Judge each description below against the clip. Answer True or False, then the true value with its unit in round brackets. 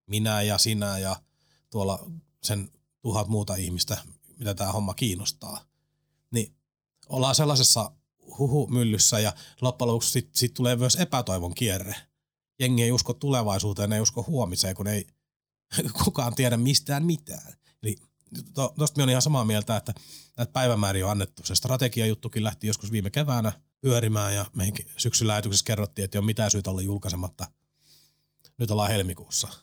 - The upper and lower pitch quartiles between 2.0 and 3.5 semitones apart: False (4.4 semitones)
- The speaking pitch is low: True (110 Hz)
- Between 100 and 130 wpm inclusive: False (150 wpm)